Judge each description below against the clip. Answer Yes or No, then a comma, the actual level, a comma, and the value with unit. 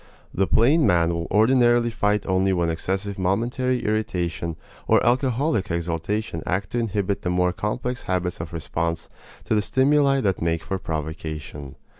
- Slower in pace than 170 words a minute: Yes, average, 150 wpm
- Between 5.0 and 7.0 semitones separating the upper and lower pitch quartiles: Yes, wide, 5.6 semitones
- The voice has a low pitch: Yes, very low, 95 Hz